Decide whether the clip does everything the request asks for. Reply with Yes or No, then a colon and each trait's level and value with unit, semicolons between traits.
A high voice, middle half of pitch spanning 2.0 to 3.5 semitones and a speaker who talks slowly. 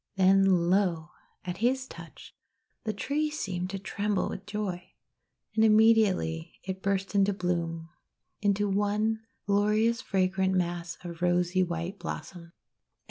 Yes: high, 195 Hz; average, 2.9 semitones; slow, 130 wpm